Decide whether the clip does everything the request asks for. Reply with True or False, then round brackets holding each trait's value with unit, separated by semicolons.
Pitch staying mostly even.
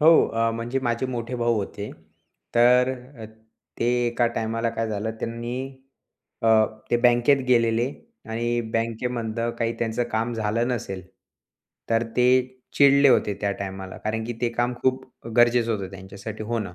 True (1.5 semitones)